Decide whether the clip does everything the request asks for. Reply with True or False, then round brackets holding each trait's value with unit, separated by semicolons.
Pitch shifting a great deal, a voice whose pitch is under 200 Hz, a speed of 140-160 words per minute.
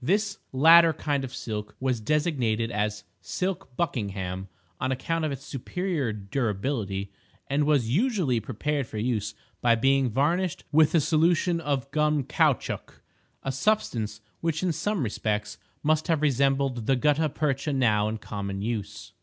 True (5.9 semitones; 135 Hz; 145 wpm)